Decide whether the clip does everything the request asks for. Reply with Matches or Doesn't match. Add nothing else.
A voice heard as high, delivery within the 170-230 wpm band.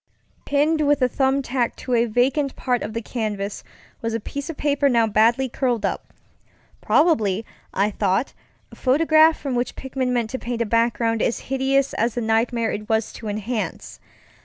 Matches